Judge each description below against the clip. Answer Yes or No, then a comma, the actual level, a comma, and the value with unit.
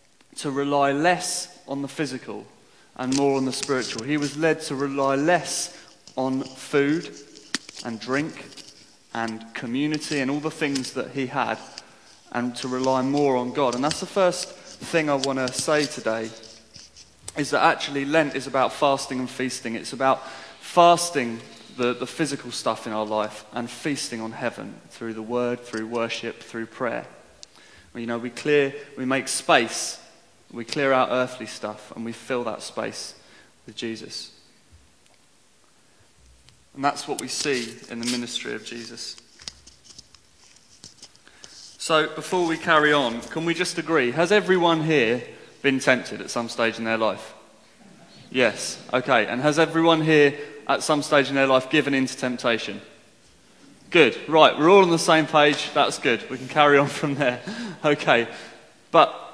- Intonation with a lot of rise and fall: No, average, 4.0 semitones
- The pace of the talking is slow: No, average, 160 wpm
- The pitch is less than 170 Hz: Yes, low, 135 Hz